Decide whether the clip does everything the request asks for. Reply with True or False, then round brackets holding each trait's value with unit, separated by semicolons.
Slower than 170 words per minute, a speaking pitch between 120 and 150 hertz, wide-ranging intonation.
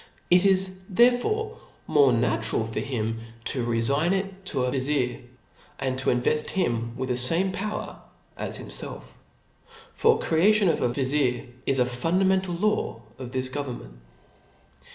True (145 wpm; 140 Hz; 7.5 semitones)